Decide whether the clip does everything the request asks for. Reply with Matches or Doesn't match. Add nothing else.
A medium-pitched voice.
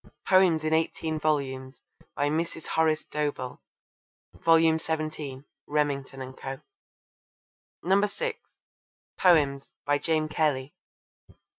Matches